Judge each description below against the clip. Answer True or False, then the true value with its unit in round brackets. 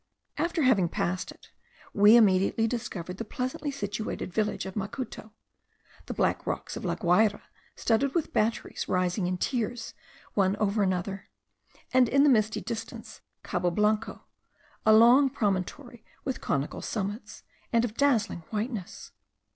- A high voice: True (215 Hz)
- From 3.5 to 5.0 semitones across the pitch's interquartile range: True (3.9 semitones)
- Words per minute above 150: False (140 wpm)